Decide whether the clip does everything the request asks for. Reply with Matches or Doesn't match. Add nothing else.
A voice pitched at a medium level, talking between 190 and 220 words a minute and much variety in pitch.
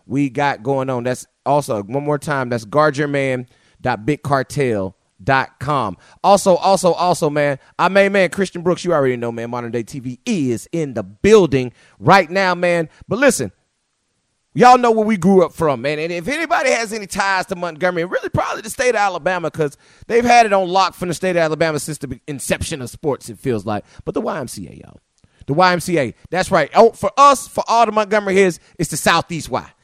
Matches